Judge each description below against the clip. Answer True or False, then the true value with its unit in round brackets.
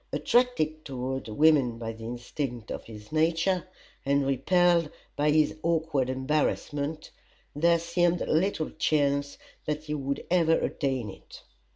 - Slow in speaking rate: True (130 wpm)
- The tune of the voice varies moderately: True (3.6 semitones)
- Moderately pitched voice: True (150 Hz)